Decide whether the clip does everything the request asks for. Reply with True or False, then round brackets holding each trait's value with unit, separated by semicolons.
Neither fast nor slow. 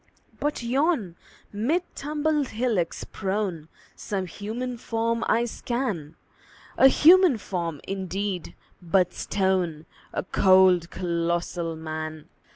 False (100 wpm)